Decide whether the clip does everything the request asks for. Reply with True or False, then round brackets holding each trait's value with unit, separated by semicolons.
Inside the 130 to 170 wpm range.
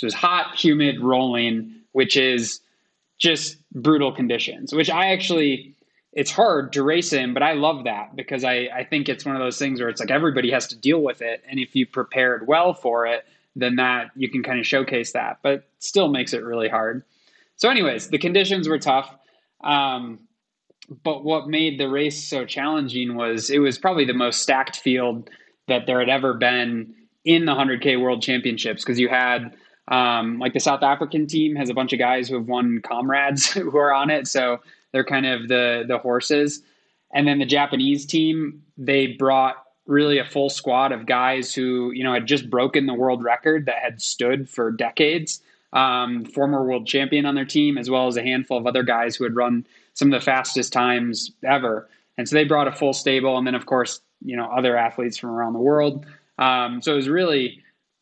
False (205 wpm)